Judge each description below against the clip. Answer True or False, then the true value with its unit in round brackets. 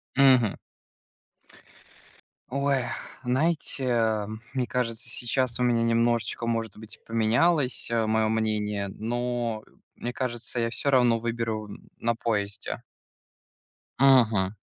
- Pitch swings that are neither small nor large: False (2.1 semitones)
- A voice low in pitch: True (115 Hz)